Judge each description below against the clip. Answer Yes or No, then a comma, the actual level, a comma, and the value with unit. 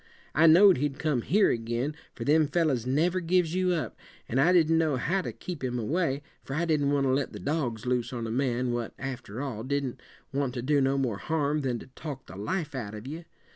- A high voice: No, medium, 140 Hz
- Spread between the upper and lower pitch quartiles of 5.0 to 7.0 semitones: No, average, 4.4 semitones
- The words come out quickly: Yes, fast, 230 wpm